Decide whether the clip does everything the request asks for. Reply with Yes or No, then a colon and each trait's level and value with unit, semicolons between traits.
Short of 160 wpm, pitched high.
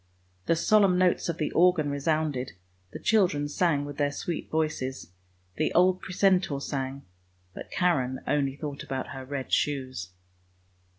No: average, 140 wpm; medium, 150 Hz